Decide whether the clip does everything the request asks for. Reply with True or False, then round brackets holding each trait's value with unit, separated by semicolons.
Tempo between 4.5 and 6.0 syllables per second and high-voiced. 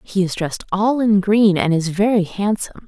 True (5.2 syllables/s; 195 Hz)